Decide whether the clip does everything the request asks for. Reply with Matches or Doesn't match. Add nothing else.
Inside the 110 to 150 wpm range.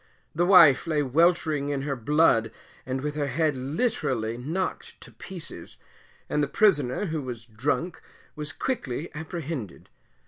Matches